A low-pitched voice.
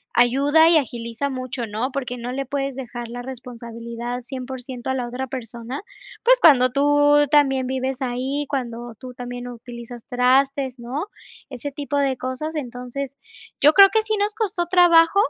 No: very high, 260 Hz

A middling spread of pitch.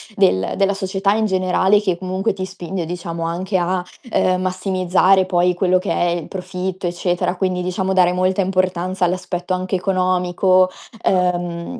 No: narrow, 1.1 semitones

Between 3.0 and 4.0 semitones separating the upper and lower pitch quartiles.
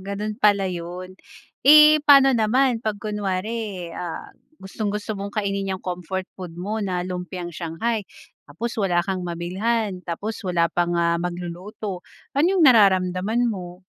Yes: average, 3.5 semitones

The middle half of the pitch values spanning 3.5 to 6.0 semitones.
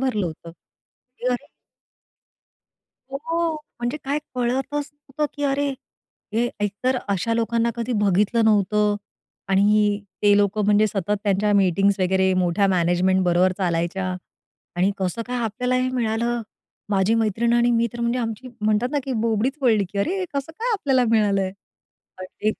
Yes: average, 4.1 semitones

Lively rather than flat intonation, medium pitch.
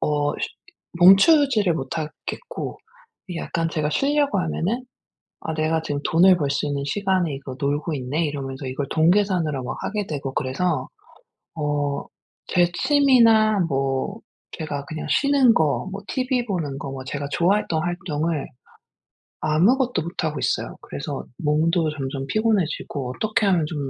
Yes: wide, 5.7 semitones; medium, 160 Hz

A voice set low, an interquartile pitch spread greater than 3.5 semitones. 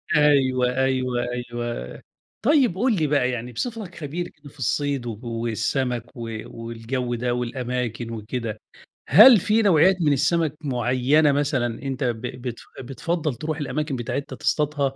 Yes: low, 130 Hz; average, 3.9 semitones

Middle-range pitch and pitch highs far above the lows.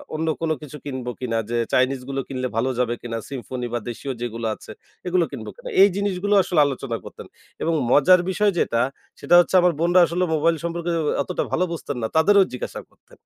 Yes: medium, 150 Hz; wide, 5.9 semitones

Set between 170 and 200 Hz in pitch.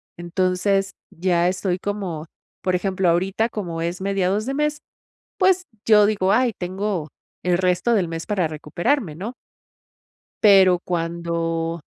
Yes: medium, 185 Hz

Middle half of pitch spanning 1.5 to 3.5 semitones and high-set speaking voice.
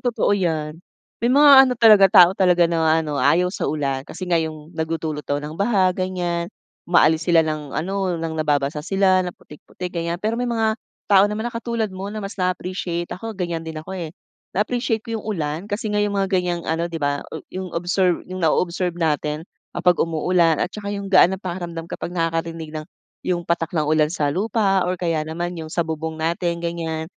No: average, 3.1 semitones; medium, 175 Hz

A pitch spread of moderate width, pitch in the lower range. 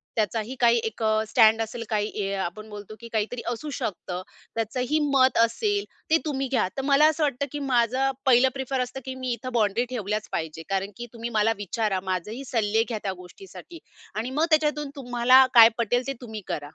No: average, 3.7 semitones; high, 235 Hz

